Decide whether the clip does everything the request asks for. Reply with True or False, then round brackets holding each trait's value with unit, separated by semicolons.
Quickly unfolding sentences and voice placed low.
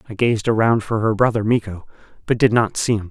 True (230 wpm; 110 Hz)